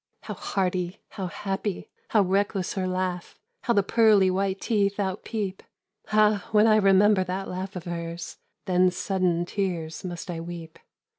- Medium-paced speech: Yes, average, 150 wpm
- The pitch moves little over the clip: Yes, narrow, 2.0 semitones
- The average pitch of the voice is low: No, high, 190 Hz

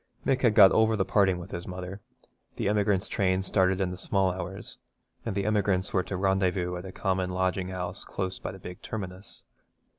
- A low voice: Yes, very low, 95 Hz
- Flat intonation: Yes, narrow, 1.3 semitones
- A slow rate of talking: No, average, 200 wpm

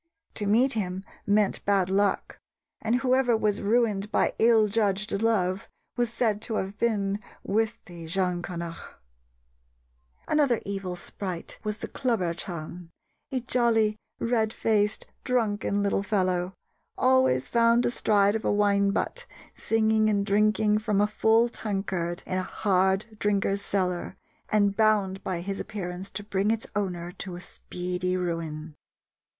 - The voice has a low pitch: No, high, 205 Hz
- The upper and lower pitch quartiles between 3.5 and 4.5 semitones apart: No, average, 2.9 semitones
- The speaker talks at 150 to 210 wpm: No, slow, 135 wpm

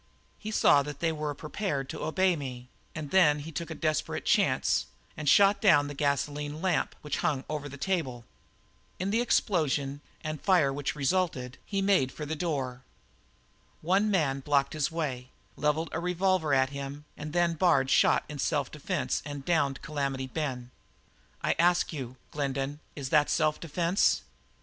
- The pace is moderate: Yes, average, 165 wpm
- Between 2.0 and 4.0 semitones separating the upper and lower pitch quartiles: Yes, average, 3.5 semitones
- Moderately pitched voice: Yes, medium, 150 Hz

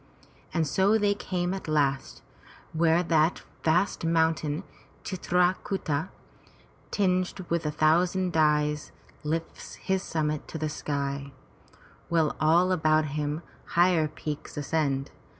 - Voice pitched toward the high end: No, medium, 160 Hz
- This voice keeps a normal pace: No, slow, 120 wpm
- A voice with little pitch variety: No, average, 3.0 semitones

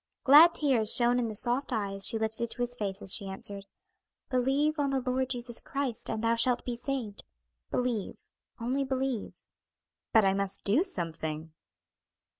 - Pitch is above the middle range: Yes, high, 240 Hz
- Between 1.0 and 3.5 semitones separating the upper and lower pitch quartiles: No, average, 4.3 semitones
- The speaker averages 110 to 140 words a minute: No, average, 165 wpm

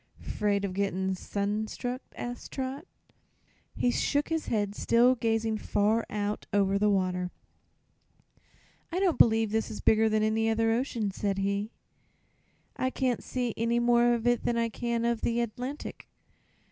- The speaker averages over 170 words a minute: No, average, 155 wpm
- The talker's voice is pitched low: No, high, 225 Hz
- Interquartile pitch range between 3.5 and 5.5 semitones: No, average, 2.8 semitones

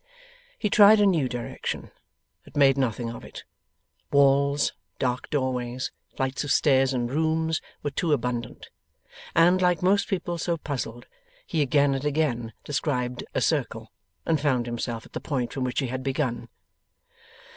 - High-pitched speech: No, low, 135 Hz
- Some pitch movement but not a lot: Yes, average, 4.1 semitones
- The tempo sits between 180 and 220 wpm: No, average, 155 wpm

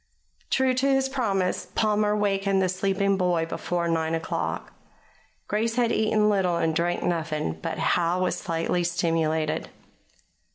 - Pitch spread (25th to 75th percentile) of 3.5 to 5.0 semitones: Yes, average, 4.1 semitones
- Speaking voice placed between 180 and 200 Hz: Yes, medium, 185 Hz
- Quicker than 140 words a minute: No, slow, 135 wpm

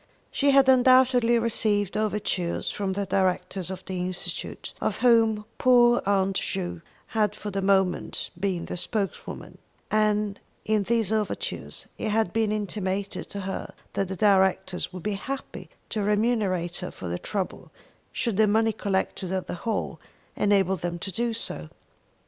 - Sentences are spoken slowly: No, average, 155 wpm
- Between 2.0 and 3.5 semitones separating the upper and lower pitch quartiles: Yes, average, 2.7 semitones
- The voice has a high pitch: Yes, high, 205 Hz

